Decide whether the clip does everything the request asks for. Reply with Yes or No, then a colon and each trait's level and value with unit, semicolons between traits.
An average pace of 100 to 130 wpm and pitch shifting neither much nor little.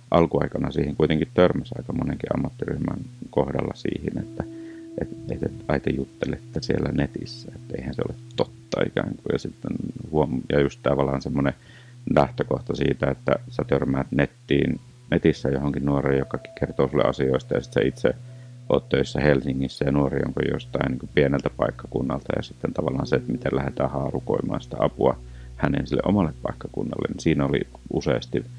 No: fast, 155 wpm; average, 3.2 semitones